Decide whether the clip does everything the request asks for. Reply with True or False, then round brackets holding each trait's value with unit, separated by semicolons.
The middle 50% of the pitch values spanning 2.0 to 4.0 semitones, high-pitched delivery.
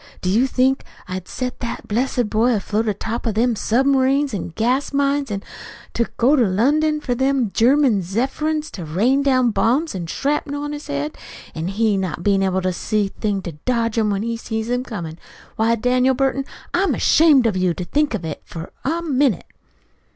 False (5.3 semitones; 235 Hz)